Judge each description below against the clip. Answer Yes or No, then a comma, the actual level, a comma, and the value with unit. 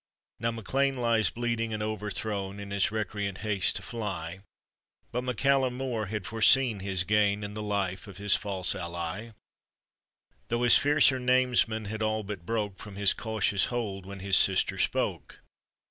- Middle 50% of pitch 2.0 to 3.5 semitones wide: Yes, average, 2.8 semitones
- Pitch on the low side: Yes, low, 105 Hz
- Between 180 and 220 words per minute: No, average, 160 wpm